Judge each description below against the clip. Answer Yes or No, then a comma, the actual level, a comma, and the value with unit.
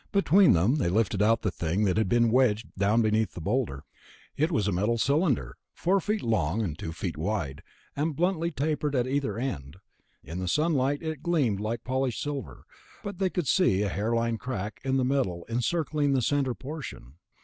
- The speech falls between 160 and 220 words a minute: Yes, average, 185 wpm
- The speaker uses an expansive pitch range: Yes, wide, 6.2 semitones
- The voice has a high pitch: No, low, 120 Hz